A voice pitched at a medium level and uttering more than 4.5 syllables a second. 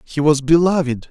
Yes: medium, 150 Hz; 5.0 syllables/s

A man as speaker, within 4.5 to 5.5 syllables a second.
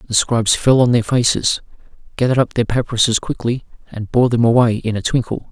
No: male; 6.1 syllables/s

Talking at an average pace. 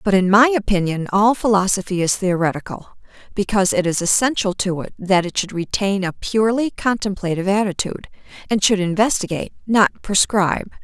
Yes: average, 150 wpm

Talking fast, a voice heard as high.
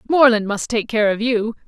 Yes: fast, 215 wpm; high, 225 Hz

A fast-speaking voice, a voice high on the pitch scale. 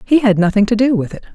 Yes: fast, 310 wpm; high, 220 Hz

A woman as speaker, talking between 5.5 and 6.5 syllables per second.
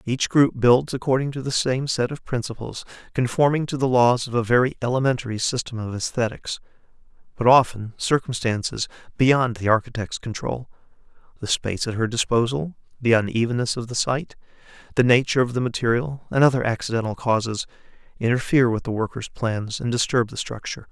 No: male; 5.7 syllables/s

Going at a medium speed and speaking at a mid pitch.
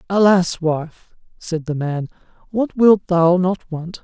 Yes: average, 150 wpm; medium, 175 Hz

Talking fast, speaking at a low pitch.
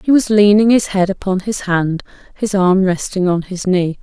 No: fast, 210 wpm; high, 190 Hz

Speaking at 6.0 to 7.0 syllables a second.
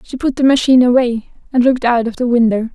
Yes: 6.6 syllables/s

